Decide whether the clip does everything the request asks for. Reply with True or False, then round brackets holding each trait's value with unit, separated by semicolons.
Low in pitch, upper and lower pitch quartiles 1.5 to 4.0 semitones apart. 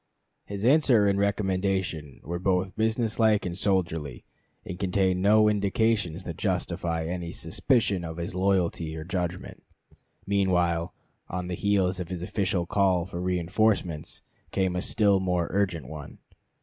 True (90 Hz; 2.7 semitones)